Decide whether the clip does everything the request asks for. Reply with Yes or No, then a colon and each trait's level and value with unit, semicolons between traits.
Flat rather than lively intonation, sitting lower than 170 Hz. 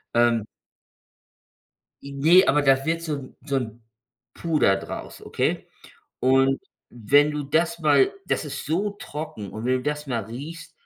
No: average, 3.8 semitones; medium, 140 Hz